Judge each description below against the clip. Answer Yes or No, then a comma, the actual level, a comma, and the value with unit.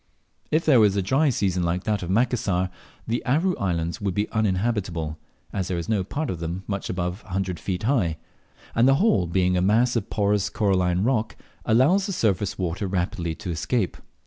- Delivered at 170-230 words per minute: Yes, average, 195 wpm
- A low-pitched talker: Yes, low, 100 Hz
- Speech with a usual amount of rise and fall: Yes, average, 4.3 semitones